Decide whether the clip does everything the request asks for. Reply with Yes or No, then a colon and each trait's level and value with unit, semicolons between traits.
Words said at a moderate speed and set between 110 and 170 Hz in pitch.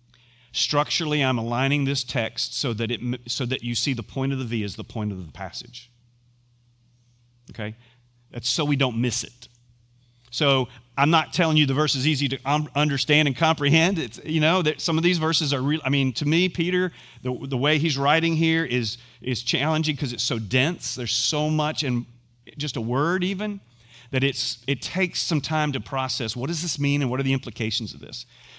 No: fast, 210 wpm; low, 130 Hz